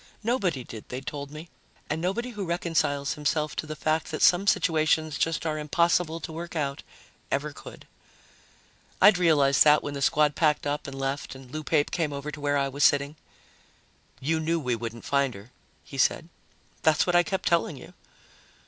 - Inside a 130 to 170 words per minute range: No, average, 185 wpm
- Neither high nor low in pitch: Yes, medium, 150 Hz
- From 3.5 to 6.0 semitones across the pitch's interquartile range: No, average, 2.8 semitones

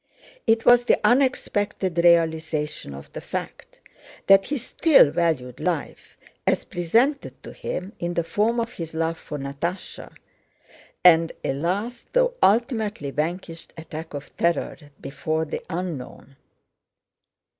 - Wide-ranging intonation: Yes, wide, 5.8 semitones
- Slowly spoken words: Yes, slow, 125 wpm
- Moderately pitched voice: Yes, medium, 170 Hz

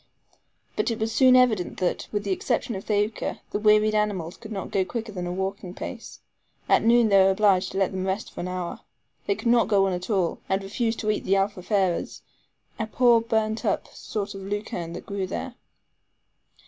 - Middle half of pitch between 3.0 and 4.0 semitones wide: No, narrow, 2.6 semitones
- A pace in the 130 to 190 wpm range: No, fast, 205 wpm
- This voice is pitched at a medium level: No, high, 205 Hz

